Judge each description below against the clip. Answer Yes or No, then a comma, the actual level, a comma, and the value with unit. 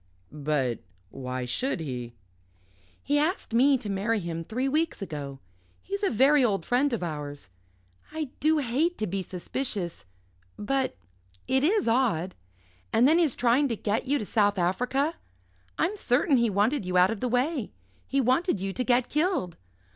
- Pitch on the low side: No, high, 235 Hz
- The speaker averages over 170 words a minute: No, average, 165 wpm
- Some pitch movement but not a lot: No, wide, 7.4 semitones